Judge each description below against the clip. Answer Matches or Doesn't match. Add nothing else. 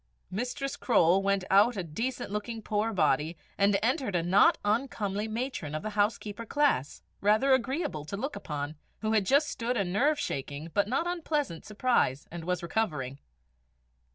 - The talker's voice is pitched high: Matches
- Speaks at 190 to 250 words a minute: Doesn't match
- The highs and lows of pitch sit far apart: Matches